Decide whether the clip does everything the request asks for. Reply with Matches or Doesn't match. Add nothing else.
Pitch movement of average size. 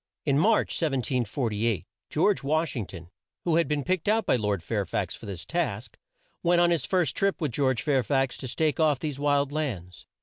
Doesn't match